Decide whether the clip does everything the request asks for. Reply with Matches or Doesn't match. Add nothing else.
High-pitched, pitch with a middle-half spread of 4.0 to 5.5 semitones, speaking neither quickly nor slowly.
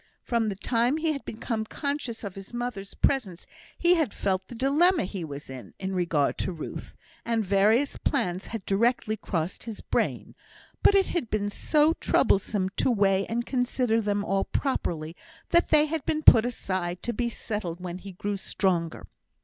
Matches